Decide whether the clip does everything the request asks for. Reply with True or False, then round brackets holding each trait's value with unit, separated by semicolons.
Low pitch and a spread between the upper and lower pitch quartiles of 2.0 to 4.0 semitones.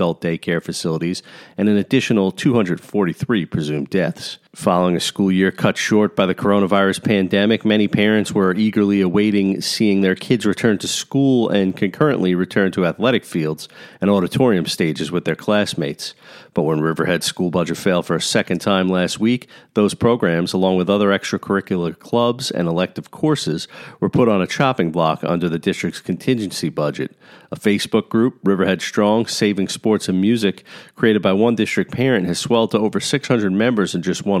True (100 Hz; 3.1 semitones)